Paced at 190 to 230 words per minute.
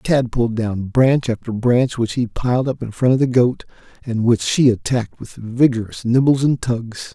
Yes: average, 200 wpm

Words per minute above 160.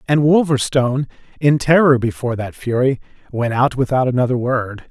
No: average, 145 wpm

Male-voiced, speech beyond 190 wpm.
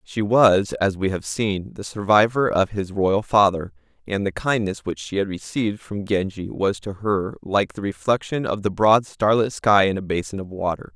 Yes: male; fast, 205 wpm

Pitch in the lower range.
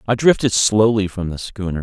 Yes: low, 105 Hz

